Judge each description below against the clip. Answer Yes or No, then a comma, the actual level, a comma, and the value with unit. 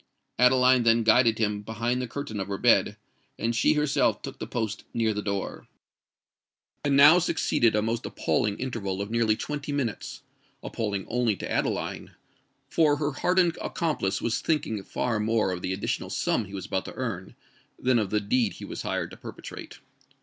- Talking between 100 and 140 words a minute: No, average, 175 wpm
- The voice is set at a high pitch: No, low, 115 Hz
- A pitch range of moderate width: Yes, average, 3.8 semitones